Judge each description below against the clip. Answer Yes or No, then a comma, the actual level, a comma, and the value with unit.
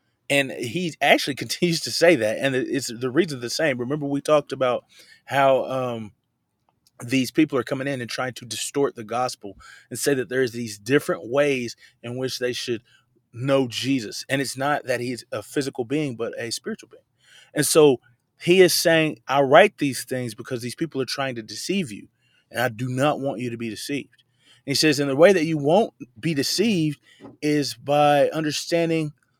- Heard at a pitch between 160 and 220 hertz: No, low, 135 Hz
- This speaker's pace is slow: No, average, 195 wpm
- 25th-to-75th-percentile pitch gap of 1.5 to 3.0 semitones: No, average, 3.4 semitones